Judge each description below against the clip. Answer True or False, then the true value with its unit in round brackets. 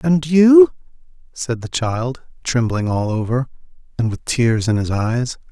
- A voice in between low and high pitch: False (120 Hz)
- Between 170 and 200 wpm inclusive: False (150 wpm)